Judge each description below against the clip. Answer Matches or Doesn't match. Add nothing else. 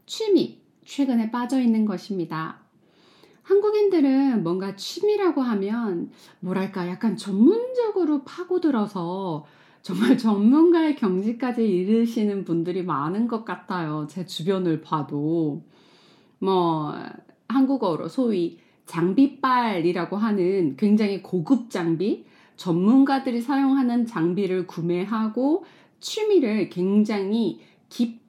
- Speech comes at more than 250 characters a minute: Doesn't match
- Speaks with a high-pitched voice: Matches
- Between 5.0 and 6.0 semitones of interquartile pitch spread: Doesn't match